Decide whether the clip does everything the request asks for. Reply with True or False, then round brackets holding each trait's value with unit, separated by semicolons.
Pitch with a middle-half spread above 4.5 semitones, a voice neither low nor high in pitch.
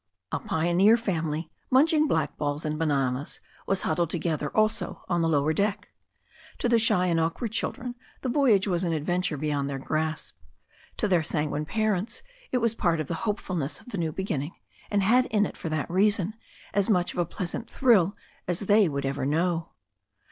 True (5.1 semitones; 175 Hz)